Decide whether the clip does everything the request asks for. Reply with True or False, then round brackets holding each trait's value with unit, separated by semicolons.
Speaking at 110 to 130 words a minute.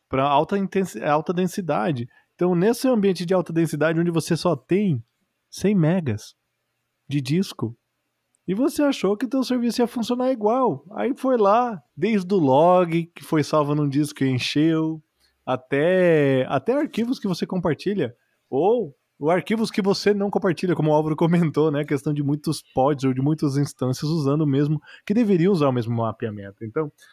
False (170 wpm)